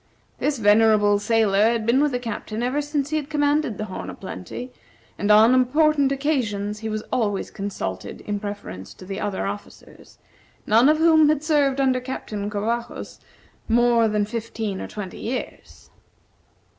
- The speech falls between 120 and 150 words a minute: No, average, 160 wpm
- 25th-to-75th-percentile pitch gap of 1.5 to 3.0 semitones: No, average, 4.8 semitones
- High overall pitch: Yes, high, 225 Hz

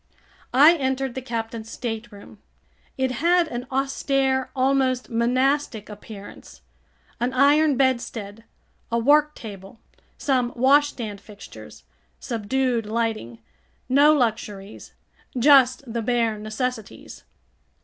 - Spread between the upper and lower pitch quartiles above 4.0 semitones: No, average, 3.2 semitones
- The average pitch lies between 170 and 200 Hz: No, high, 245 Hz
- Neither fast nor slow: No, slow, 95 wpm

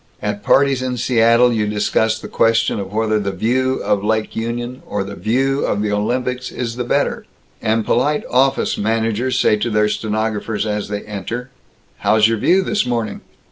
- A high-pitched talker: No, low, 115 Hz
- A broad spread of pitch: No, average, 2.8 semitones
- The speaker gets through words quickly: No, average, 180 wpm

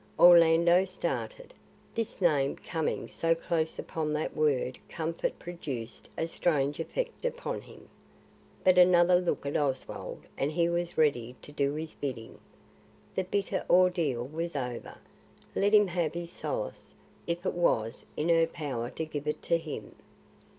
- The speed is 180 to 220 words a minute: No, average, 150 wpm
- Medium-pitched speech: Yes, medium, 165 Hz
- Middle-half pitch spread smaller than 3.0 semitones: No, average, 3.4 semitones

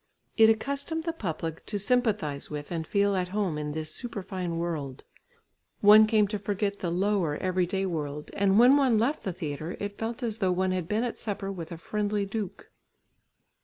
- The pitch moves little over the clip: No, average, 4.3 semitones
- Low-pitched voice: No, high, 195 Hz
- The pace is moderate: Yes, average, 185 wpm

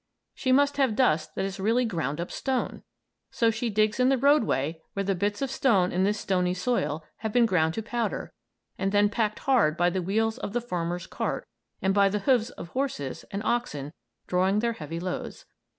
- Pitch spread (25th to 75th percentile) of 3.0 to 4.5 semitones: No, average, 5.1 semitones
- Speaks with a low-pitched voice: No, high, 205 Hz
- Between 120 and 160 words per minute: No, average, 200 wpm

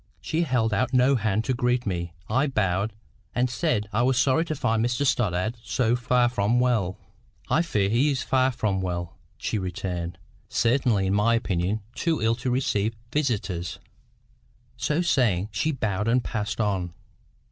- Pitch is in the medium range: No, low, 115 Hz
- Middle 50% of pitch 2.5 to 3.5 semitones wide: No, average, 4.3 semitones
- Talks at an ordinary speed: Yes, average, 165 wpm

